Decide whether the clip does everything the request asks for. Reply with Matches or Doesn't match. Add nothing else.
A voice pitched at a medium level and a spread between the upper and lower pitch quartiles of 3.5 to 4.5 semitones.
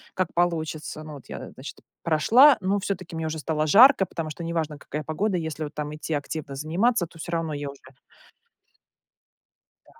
Doesn't match